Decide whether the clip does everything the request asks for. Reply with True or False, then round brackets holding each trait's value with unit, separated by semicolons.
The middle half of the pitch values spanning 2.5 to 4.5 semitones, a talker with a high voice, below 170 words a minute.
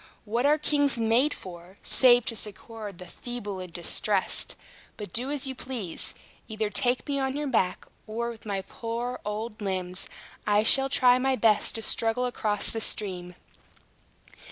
True (3.6 semitones; 225 Hz; 160 wpm)